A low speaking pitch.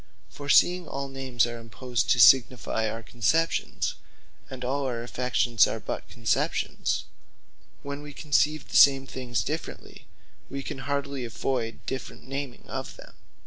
Yes: low, 130 Hz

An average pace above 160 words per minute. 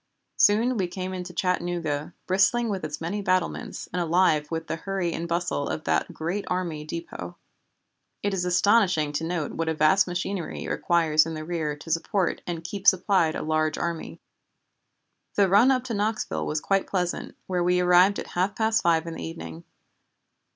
Yes: average, 180 wpm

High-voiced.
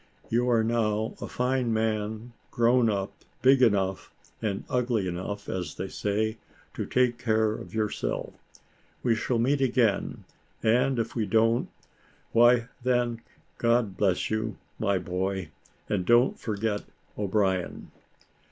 No: low, 110 Hz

